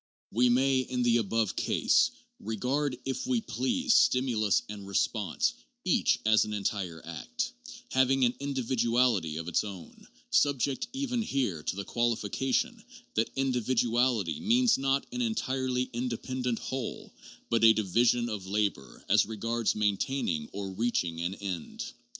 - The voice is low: Yes, low, 120 Hz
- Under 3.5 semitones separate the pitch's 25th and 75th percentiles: No, average, 4.4 semitones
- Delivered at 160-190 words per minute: No, average, 140 wpm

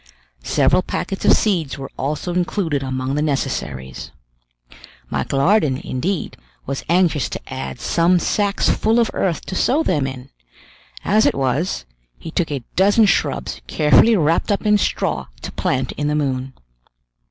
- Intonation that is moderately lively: No, wide, 6.2 semitones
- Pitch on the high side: No, medium, 155 Hz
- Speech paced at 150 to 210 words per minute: Yes, average, 155 wpm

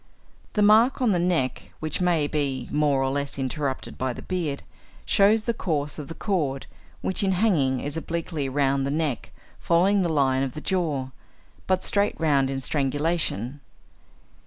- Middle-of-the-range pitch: Yes, medium, 150 Hz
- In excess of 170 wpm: No, average, 165 wpm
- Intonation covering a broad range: No, average, 4.9 semitones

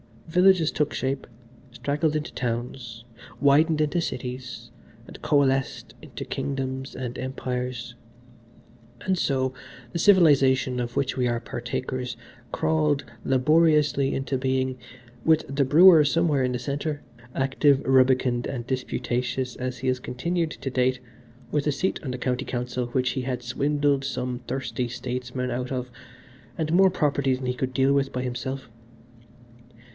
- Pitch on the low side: Yes, low, 130 Hz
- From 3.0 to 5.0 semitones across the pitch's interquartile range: No, narrow, 2.5 semitones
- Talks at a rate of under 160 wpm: Yes, average, 140 wpm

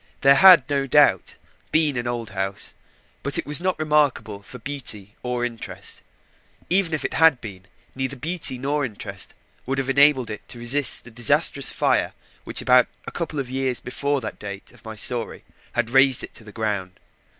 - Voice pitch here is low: Yes, low, 125 Hz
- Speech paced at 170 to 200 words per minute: Yes, average, 180 wpm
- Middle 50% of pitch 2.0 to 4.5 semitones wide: Yes, average, 4.2 semitones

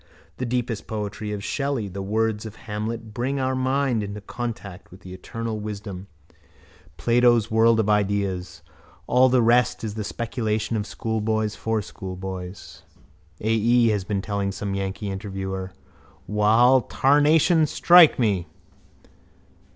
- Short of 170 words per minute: Yes, slow, 135 wpm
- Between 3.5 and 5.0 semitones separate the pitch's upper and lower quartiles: No, average, 3.1 semitones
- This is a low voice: Yes, low, 110 Hz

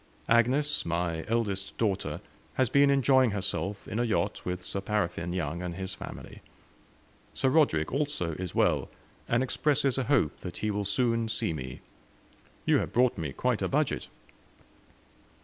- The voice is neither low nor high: No, low, 105 Hz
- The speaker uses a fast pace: No, average, 155 wpm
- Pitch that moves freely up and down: Yes, wide, 6.2 semitones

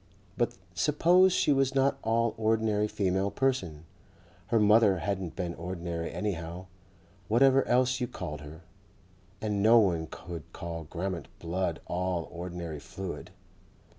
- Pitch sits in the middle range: No, very low, 95 Hz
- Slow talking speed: Yes, slow, 130 wpm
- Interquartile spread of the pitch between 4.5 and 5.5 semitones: Yes, average, 5.0 semitones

